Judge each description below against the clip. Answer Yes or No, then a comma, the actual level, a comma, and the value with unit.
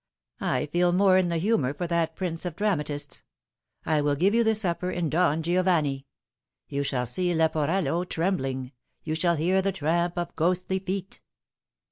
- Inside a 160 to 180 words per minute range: Yes, average, 170 wpm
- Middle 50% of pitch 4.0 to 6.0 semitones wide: No, average, 3.3 semitones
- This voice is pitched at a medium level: Yes, medium, 170 Hz